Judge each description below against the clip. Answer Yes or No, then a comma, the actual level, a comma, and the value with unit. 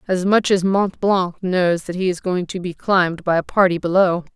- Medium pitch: Yes, medium, 180 Hz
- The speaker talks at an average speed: No, fast, 235 wpm